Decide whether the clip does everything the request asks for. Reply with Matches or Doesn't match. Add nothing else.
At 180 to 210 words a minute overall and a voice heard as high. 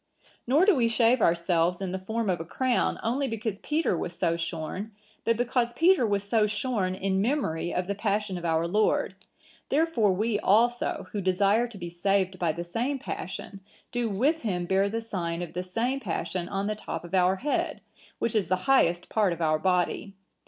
Matches